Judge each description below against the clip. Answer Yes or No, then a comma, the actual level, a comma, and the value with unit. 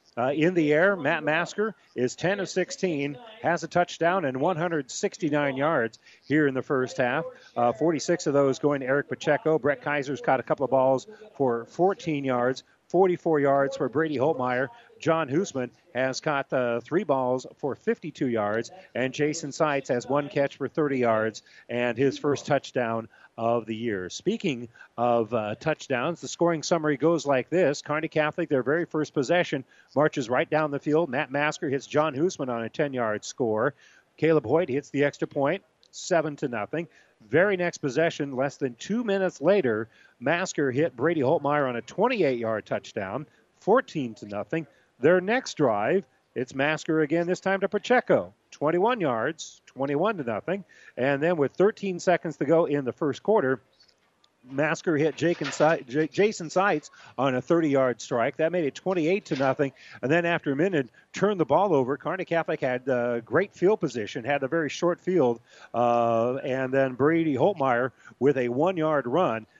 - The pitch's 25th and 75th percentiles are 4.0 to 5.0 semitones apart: Yes, average, 4.3 semitones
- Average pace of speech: Yes, average, 175 wpm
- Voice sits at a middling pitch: Yes, medium, 150 Hz